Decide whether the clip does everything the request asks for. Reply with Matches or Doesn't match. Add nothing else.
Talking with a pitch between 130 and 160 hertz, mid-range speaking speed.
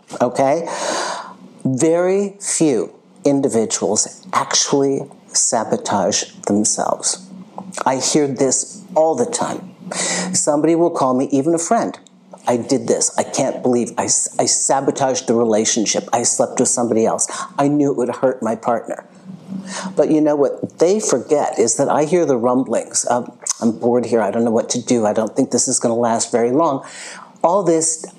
Matches